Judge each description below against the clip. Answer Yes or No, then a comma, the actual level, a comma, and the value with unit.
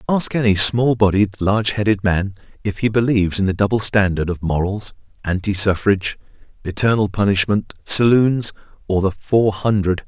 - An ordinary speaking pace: Yes, average, 150 wpm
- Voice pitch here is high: No, low, 100 Hz